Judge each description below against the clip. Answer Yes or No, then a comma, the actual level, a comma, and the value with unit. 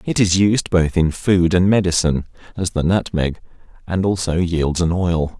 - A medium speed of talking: Yes, average, 180 wpm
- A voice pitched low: Yes, very low, 90 Hz